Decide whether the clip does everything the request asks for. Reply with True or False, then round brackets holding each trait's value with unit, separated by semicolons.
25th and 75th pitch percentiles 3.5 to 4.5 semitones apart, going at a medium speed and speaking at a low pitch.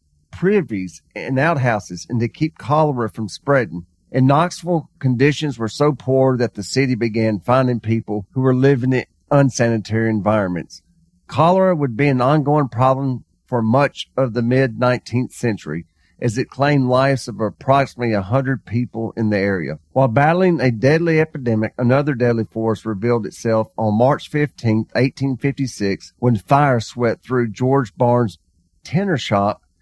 True (4.0 semitones; 155 wpm; 125 Hz)